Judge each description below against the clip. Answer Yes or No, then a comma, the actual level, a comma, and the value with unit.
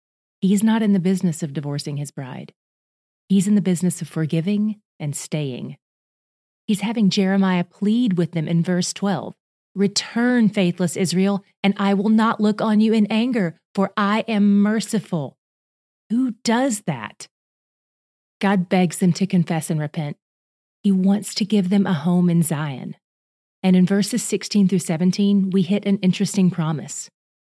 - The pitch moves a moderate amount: Yes, average, 3.3 semitones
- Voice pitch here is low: No, high, 190 Hz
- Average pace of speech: Yes, average, 155 wpm